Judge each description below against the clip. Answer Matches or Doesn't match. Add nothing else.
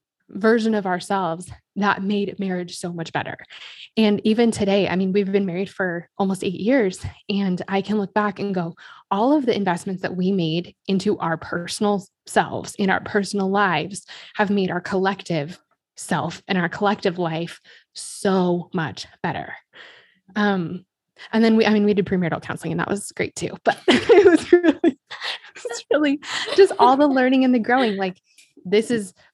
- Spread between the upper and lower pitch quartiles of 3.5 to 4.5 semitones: Doesn't match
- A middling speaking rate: Matches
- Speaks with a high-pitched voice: Matches